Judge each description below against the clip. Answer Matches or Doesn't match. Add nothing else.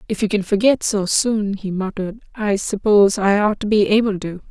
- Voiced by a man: Doesn't match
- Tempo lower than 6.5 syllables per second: Matches